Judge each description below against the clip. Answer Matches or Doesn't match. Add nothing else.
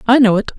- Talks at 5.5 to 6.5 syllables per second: Doesn't match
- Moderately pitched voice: Doesn't match